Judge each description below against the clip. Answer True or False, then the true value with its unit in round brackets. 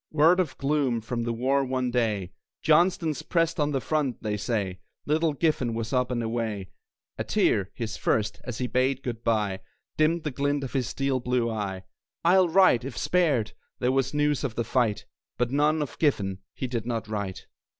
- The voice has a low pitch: True (125 Hz)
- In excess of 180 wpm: True (190 wpm)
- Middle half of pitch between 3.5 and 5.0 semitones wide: True (4.6 semitones)